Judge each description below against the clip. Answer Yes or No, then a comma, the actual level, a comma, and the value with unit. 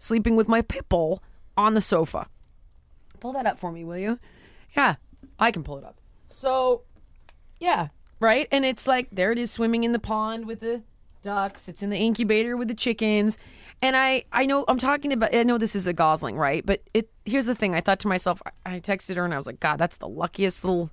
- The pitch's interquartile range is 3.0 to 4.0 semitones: No, average, 4.7 semitones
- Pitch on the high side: Yes, high, 215 Hz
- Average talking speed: No, fast, 225 wpm